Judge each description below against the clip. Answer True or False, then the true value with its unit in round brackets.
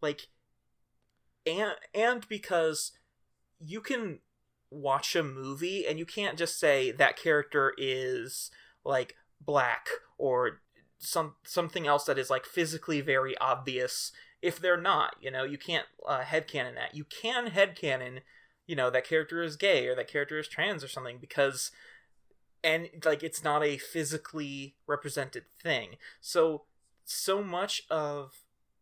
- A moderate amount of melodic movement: False (5.8 semitones)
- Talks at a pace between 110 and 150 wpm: True (140 wpm)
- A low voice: False (160 Hz)